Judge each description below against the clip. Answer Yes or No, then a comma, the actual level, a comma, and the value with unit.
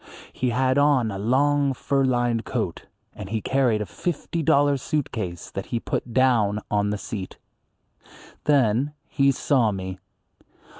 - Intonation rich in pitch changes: No, average, 4.8 semitones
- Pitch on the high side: No, low, 125 Hz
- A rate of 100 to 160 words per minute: Yes, average, 150 wpm